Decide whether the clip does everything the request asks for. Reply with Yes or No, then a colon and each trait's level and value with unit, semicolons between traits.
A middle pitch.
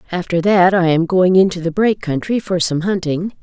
Yes: medium, 180 Hz